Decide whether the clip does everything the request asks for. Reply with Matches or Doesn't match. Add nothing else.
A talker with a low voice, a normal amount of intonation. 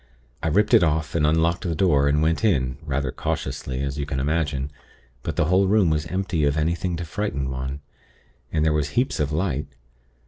Matches